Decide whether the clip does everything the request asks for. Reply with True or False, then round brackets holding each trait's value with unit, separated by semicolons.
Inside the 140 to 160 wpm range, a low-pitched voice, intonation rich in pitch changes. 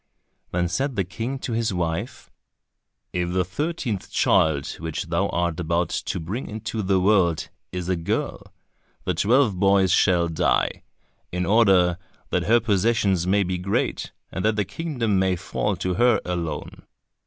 False (155 wpm; 95 Hz; 3.8 semitones)